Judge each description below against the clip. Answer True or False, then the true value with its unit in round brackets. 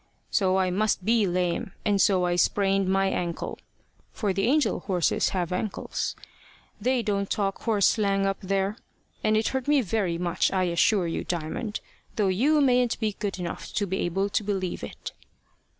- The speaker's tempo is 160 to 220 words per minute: True (175 wpm)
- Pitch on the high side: True (195 Hz)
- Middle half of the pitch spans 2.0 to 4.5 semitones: True (2.8 semitones)